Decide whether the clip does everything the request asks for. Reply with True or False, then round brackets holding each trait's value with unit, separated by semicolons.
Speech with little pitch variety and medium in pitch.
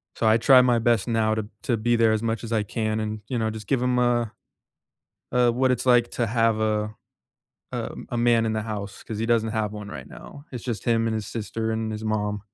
False (1.7 semitones; 115 Hz)